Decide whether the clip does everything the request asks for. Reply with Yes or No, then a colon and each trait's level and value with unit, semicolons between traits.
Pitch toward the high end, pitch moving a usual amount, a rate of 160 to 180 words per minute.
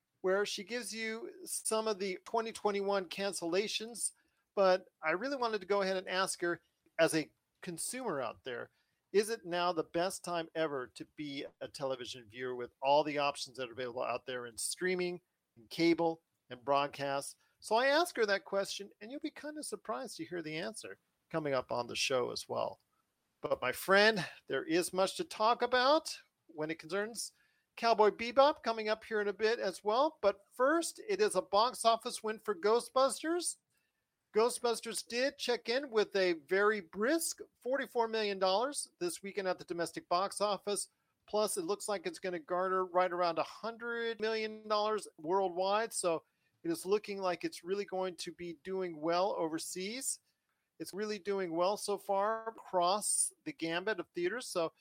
Yes: high, 200 Hz; average, 4.7 semitones; average, 175 wpm